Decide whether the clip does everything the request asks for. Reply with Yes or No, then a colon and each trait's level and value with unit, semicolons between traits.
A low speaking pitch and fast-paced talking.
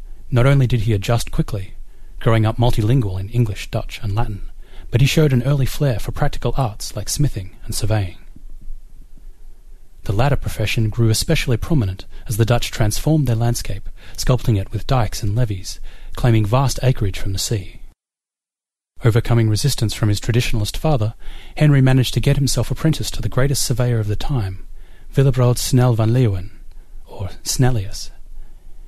No: low, 115 Hz; average, 160 wpm